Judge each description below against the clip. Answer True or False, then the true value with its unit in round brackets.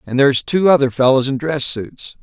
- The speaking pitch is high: False (135 Hz)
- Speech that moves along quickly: True (215 wpm)